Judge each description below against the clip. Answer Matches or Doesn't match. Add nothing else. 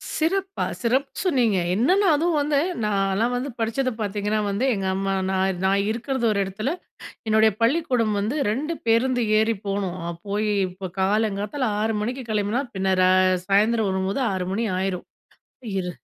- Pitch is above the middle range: Matches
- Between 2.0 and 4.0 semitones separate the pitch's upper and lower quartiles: Doesn't match